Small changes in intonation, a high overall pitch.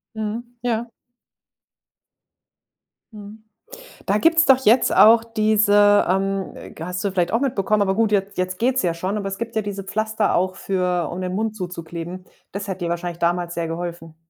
No: average, 3.3 semitones; high, 195 Hz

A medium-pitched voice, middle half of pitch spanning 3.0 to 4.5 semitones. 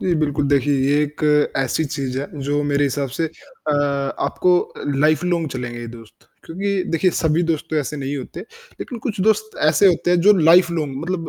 Yes: medium, 155 Hz; average, 3.8 semitones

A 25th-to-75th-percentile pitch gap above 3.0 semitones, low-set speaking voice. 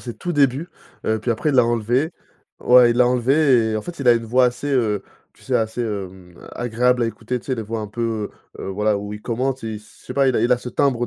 No: narrow, 2.6 semitones; low, 120 Hz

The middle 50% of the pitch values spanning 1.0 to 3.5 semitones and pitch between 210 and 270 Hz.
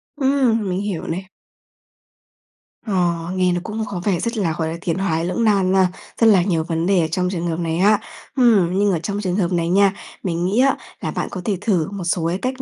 No: average, 3.1 semitones; medium, 185 Hz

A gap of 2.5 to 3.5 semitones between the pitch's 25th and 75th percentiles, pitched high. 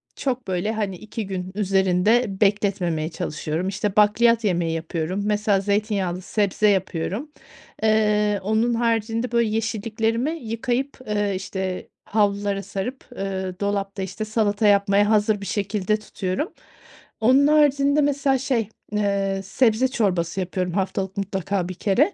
Yes: average, 2.8 semitones; high, 205 Hz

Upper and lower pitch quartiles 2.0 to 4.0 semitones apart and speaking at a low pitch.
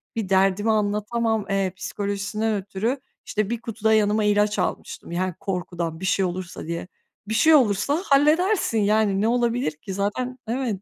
No: average, 3.0 semitones; high, 210 Hz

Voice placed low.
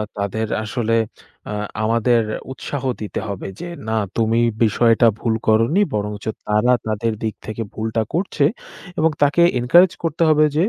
Yes: low, 115 Hz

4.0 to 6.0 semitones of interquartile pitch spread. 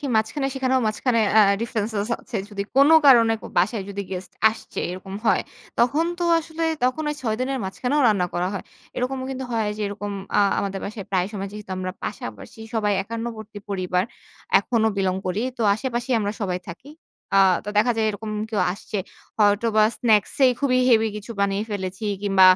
No: average, 3.5 semitones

